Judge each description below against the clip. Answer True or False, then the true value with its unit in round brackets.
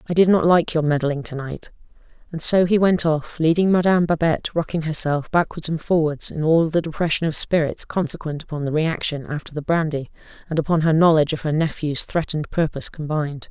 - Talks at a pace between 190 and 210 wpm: True (195 wpm)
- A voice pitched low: False (160 Hz)